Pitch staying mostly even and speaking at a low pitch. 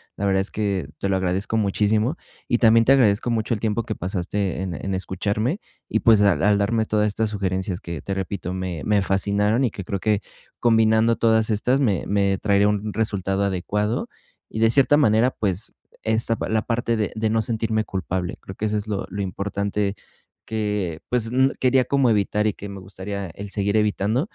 Yes: narrow, 2.3 semitones; low, 105 Hz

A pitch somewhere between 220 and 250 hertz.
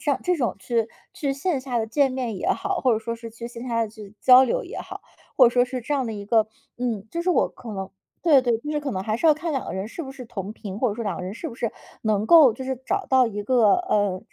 Yes: high, 240 Hz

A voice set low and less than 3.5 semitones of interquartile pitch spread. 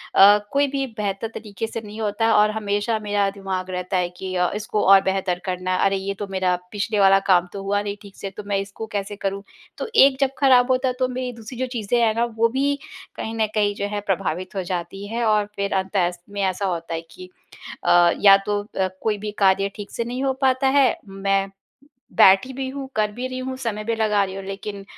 No: high, 205 Hz; average, 2.8 semitones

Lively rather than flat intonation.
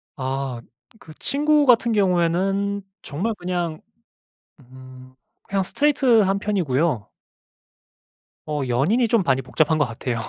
Yes: wide, 7.7 semitones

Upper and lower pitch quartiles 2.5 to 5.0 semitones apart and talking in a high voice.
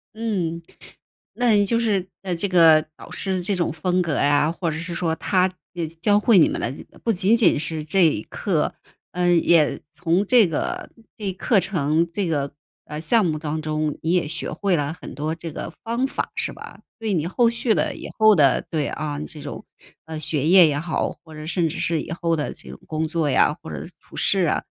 No: average, 3.6 semitones; medium, 170 Hz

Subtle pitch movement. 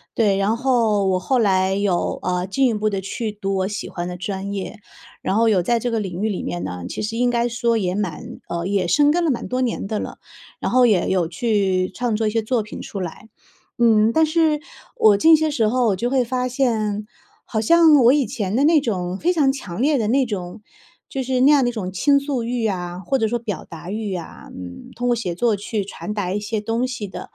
No: average, 4.3 semitones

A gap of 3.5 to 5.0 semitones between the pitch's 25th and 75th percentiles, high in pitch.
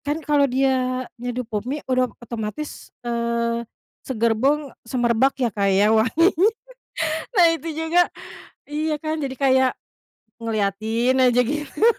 Yes: average, 4.1 semitones; very high, 255 Hz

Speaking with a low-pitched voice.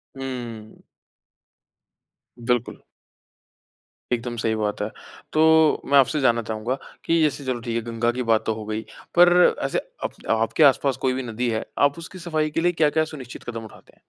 Yes: low, 125 Hz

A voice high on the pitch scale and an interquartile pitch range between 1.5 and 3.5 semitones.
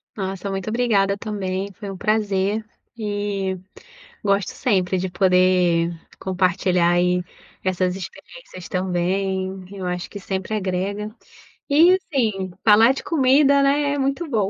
Yes: high, 195 Hz; average, 2.8 semitones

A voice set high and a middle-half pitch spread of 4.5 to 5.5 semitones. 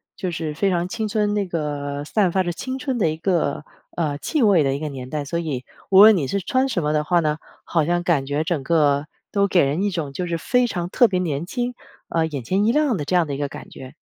No: medium, 170 Hz; average, 5.1 semitones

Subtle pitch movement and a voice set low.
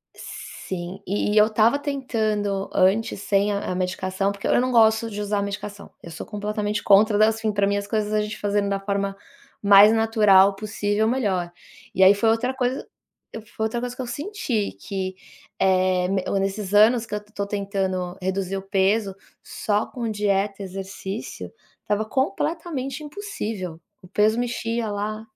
No: narrow, 2.2 semitones; high, 205 Hz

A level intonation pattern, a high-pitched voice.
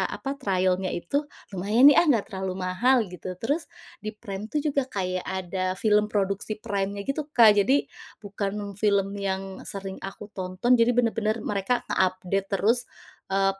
No: average, 3.1 semitones; high, 200 Hz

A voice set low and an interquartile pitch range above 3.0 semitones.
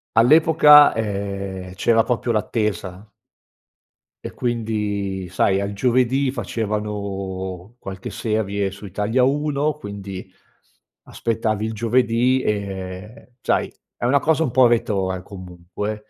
Yes: low, 105 Hz; average, 3.7 semitones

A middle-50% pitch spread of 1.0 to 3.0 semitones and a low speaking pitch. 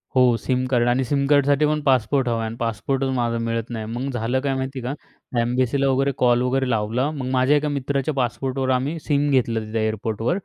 Yes: average, 2.7 semitones; low, 130 Hz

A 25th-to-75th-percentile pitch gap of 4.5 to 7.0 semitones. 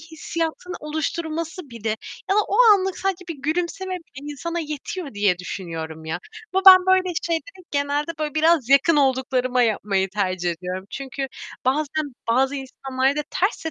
Yes: average, 5.3 semitones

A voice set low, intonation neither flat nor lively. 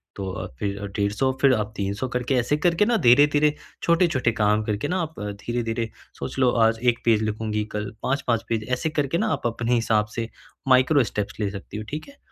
Yes: low, 115 Hz; average, 4.6 semitones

